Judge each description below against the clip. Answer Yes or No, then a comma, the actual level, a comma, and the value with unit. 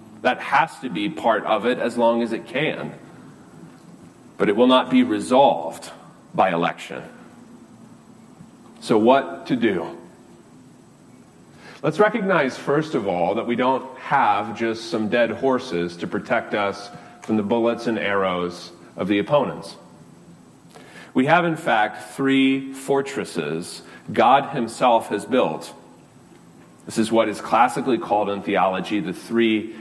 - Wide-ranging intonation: Yes, wide, 5.9 semitones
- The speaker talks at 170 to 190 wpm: No, slow, 135 wpm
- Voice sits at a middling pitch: No, low, 110 Hz